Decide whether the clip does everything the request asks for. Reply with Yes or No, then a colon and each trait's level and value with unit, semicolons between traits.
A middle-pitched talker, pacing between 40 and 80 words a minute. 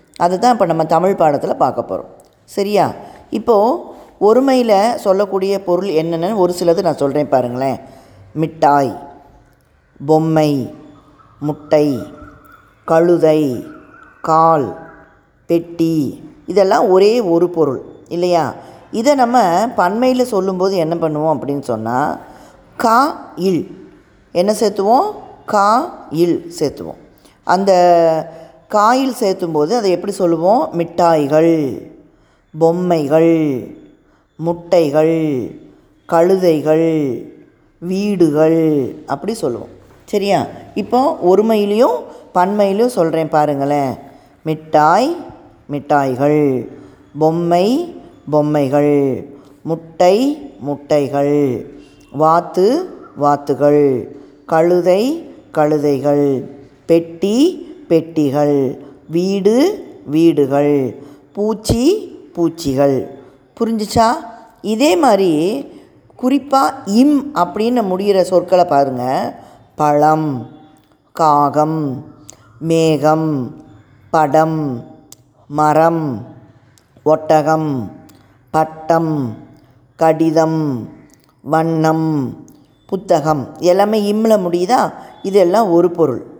Yes: medium, 160 Hz; slow, 75 wpm